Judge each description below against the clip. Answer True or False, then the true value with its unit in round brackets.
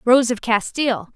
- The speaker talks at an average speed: True (155 wpm)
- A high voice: True (235 Hz)